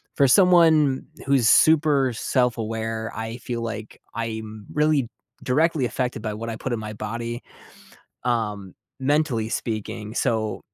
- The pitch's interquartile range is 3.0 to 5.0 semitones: Yes, average, 3.6 semitones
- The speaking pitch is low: Yes, low, 115 Hz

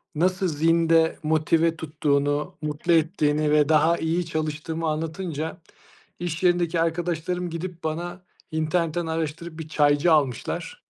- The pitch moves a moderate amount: No, narrow, 1.8 semitones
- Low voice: No, medium, 160 Hz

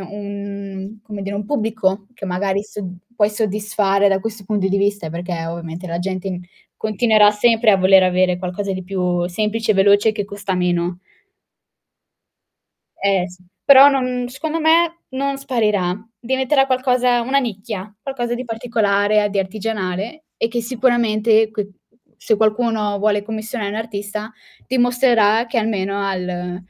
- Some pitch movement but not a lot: Yes, average, 3.2 semitones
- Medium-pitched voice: No, high, 210 Hz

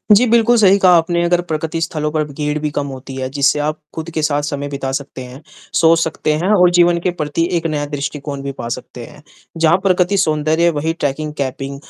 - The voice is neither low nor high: Yes, medium, 155 Hz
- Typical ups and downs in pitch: Yes, average, 3.1 semitones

